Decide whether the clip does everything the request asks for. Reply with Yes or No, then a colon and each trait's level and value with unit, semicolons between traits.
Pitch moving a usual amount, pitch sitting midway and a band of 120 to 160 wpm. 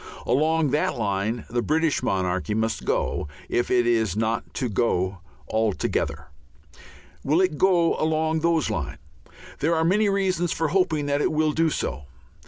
No: wide, 6.6 semitones; medium, 150 Hz; average, 155 wpm